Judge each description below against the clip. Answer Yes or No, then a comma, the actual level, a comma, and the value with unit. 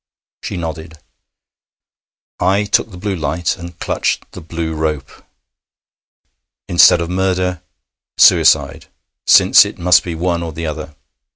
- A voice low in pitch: Yes, very low, 85 Hz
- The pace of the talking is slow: Yes, slow, 125 wpm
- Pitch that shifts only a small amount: Yes, narrow, 2.1 semitones